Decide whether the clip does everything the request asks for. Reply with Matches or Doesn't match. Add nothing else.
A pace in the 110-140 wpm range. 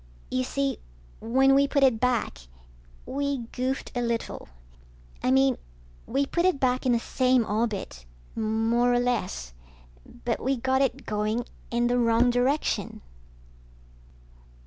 Matches